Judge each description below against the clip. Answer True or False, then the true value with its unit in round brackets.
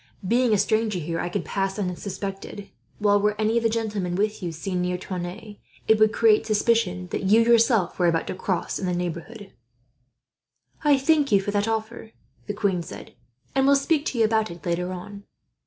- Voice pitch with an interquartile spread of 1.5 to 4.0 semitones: True (3.6 semitones)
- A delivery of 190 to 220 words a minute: True (195 wpm)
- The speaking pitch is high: True (205 Hz)